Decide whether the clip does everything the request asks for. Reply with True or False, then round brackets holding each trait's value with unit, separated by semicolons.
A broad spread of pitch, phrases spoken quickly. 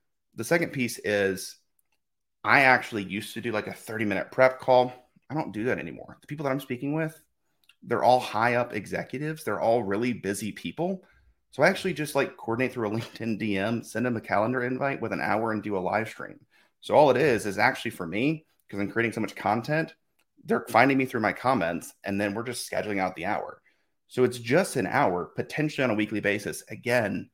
False (4.3 semitones; 215 wpm)